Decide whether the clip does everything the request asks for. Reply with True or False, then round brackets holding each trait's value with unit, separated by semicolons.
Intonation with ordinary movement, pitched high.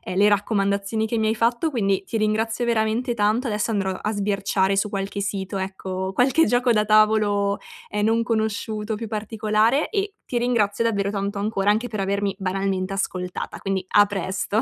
False (2.2 semitones; 210 Hz)